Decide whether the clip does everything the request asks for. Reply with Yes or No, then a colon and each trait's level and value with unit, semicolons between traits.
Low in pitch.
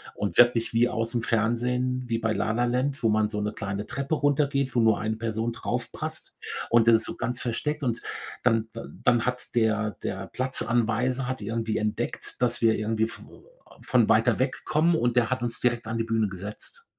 Yes: low, 115 Hz